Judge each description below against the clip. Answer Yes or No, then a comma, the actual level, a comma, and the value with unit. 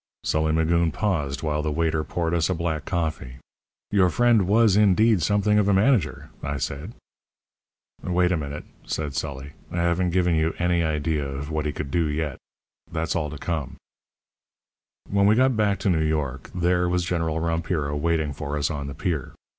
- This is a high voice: No, very low, 80 Hz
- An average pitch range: Yes, average, 3.2 semitones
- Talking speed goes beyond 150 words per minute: Yes, average, 180 wpm